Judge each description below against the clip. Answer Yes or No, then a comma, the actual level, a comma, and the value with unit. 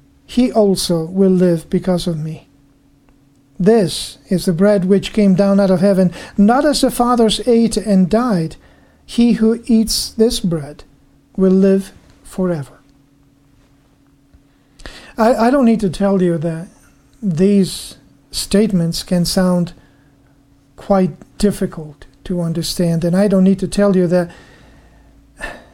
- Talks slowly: Yes, slow, 130 wpm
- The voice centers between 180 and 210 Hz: Yes, medium, 185 Hz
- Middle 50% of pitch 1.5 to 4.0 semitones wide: No, average, 4.4 semitones